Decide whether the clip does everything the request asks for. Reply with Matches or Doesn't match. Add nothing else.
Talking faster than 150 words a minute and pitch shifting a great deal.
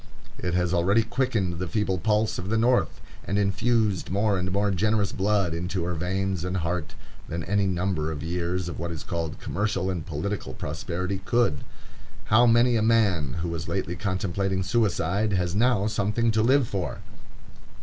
Doesn't match